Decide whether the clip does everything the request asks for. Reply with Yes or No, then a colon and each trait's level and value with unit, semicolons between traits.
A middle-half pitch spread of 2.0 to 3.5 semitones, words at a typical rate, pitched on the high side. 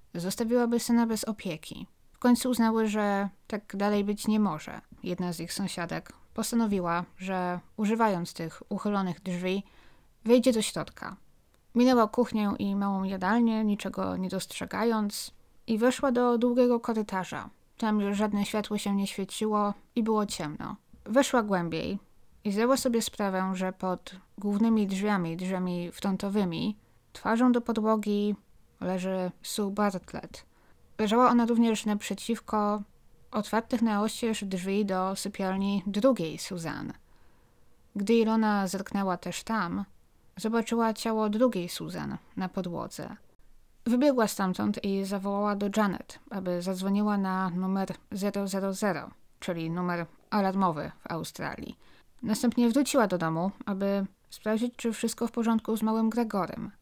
Yes: average, 2.8 semitones; average, 125 wpm; high, 205 Hz